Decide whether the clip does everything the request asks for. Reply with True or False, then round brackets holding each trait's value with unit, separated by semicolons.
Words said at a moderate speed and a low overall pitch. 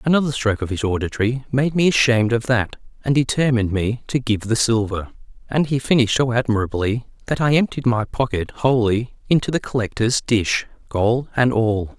True (175 wpm; 120 Hz)